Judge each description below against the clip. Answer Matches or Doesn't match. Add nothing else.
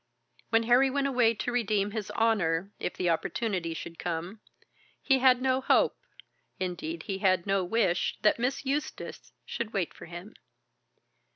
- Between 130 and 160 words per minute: Matches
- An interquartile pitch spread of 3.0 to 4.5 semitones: Doesn't match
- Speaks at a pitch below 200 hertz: Doesn't match